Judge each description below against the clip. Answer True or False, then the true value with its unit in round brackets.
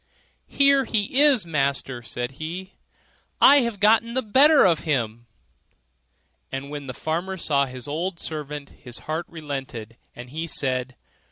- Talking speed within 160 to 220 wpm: False (145 wpm)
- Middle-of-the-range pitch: True (155 Hz)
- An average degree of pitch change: False (6.9 semitones)